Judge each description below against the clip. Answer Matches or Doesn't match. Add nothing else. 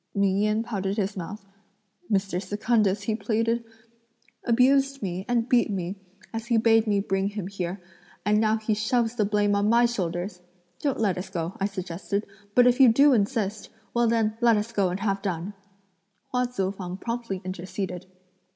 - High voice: Matches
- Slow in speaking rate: Doesn't match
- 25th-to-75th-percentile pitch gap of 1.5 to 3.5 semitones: Matches